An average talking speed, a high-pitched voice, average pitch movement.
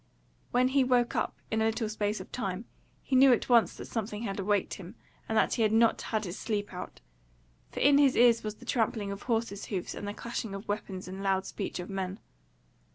No: fast, 220 wpm; high, 215 Hz; average, 3.1 semitones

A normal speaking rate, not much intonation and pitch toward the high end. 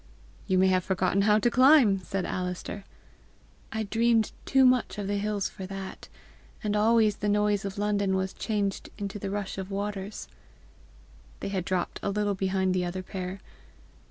Yes: average, 170 wpm; narrow, 1.7 semitones; high, 200 Hz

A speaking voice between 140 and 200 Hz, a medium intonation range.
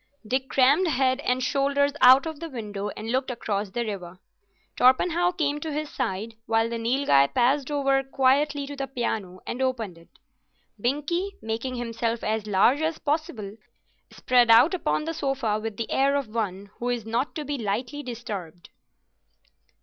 No: very high, 255 Hz; average, 4.3 semitones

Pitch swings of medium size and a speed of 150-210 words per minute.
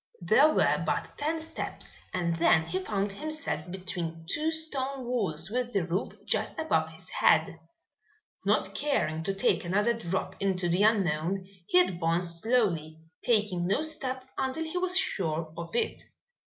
No: wide, 7.3 semitones; average, 155 wpm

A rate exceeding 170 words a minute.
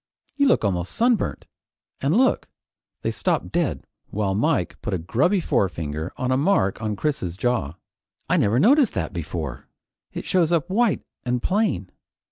No: average, 160 wpm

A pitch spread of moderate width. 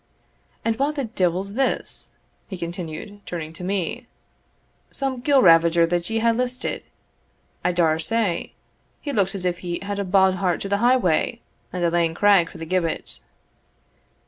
Yes: average, 4.7 semitones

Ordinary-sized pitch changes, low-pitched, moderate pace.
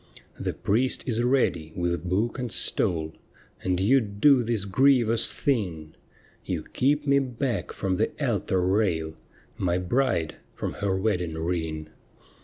No: wide, 6.1 semitones; low, 100 Hz; average, 145 wpm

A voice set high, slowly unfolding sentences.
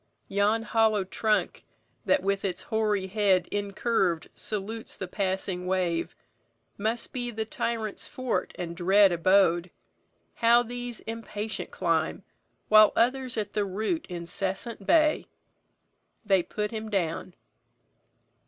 Yes: high, 205 Hz; slow, 115 wpm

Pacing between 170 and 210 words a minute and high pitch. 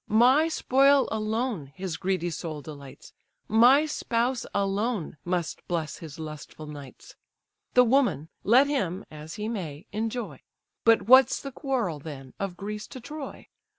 No: average, 140 wpm; high, 210 Hz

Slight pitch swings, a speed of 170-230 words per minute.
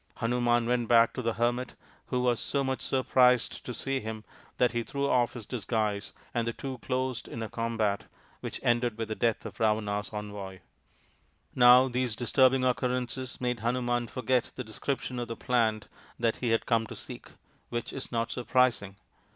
Yes: narrow, 2.0 semitones; average, 175 wpm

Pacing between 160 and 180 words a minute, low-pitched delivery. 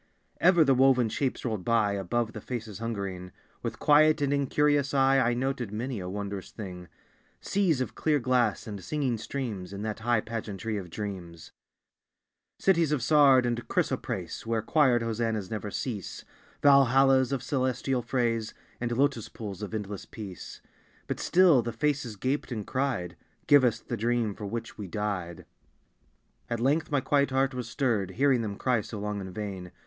Yes: average, 165 wpm; low, 120 Hz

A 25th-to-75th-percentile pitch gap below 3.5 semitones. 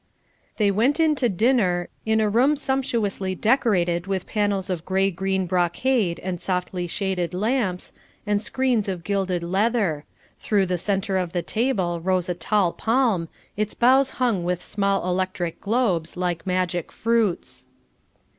No: average, 3.9 semitones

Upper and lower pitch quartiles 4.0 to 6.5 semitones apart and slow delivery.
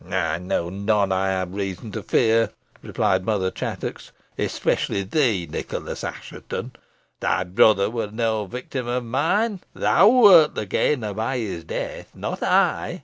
No: average, 4.5 semitones; average, 145 wpm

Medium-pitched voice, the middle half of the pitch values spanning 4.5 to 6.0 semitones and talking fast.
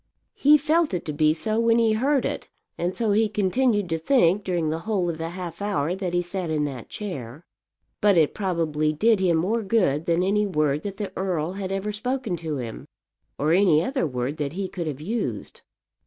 Yes: medium, 180 Hz; average, 5.0 semitones; fast, 210 wpm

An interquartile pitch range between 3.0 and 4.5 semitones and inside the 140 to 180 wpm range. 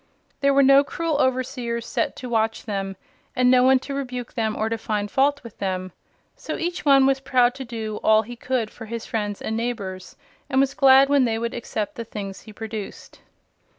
No: average, 3.5 semitones; fast, 205 wpm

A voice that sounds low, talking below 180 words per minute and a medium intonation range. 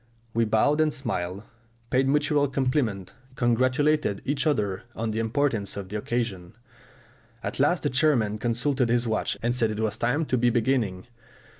Yes: low, 120 Hz; average, 160 wpm; average, 4.6 semitones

